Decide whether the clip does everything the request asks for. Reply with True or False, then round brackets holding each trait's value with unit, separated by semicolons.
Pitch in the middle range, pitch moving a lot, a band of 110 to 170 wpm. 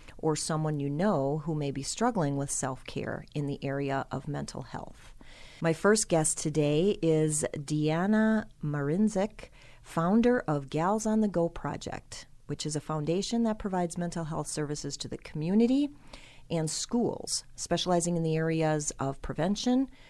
False (155 Hz; 4.7 semitones; 150 wpm)